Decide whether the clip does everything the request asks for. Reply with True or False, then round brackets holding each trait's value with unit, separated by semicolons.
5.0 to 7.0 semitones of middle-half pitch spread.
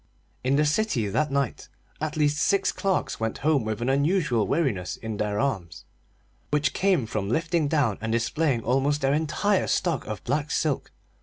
True (5.3 semitones)